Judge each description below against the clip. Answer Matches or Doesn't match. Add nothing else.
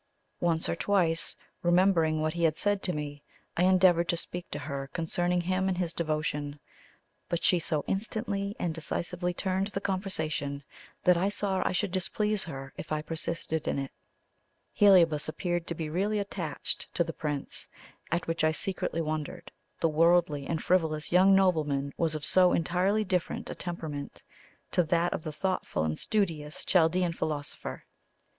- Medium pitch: Matches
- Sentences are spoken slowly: Doesn't match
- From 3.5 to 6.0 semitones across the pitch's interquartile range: Doesn't match